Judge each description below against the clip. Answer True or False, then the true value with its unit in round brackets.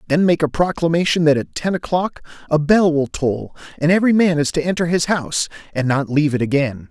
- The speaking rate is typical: False (215 wpm)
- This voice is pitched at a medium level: True (155 Hz)